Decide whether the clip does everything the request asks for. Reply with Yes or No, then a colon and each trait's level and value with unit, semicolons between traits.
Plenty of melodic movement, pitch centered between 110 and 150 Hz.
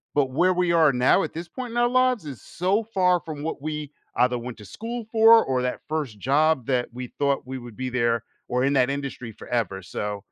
Yes: wide, 6.3 semitones; medium, 140 Hz